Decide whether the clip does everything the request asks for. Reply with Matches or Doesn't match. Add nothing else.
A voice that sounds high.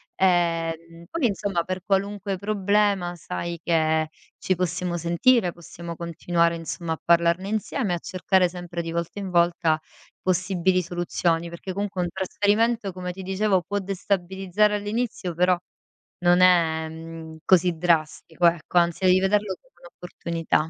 Doesn't match